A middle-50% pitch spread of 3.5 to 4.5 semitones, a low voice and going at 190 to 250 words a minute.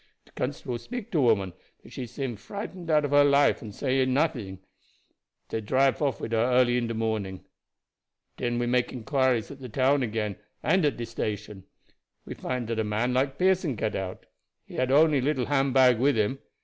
Yes: average, 3.9 semitones; low, 125 Hz; average, 200 wpm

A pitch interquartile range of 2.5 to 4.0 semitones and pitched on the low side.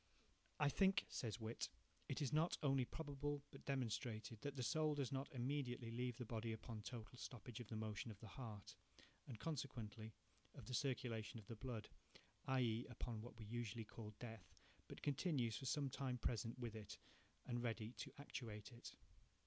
Yes: average, 3.4 semitones; low, 120 Hz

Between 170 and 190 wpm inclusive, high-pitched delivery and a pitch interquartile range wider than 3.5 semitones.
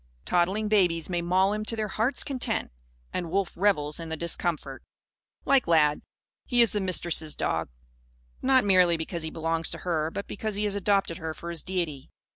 No: average, 185 wpm; medium, 175 Hz; average, 4.0 semitones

